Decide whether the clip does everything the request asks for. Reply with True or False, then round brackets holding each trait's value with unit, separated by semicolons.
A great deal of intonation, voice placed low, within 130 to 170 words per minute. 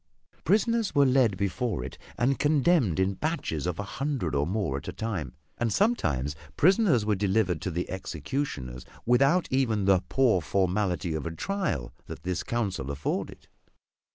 True (8.2 semitones; 105 Hz; 155 wpm)